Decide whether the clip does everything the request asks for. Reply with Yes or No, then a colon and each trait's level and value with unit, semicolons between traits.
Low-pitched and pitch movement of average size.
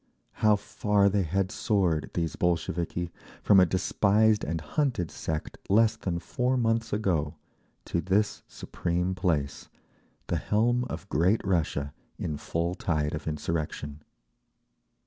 Yes: very low, 90 Hz; average, 4.4 semitones